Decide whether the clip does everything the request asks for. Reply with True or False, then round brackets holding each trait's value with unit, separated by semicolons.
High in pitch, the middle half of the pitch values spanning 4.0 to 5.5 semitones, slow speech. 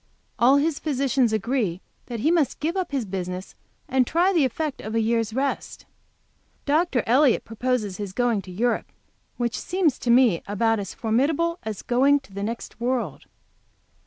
False (245 Hz; 4.5 semitones; 165 wpm)